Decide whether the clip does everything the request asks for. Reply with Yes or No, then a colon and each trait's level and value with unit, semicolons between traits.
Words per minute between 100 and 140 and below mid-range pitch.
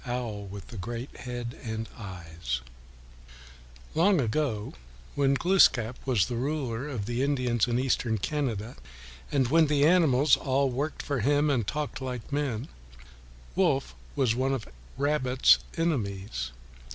Yes: slow, 135 wpm; low, 125 Hz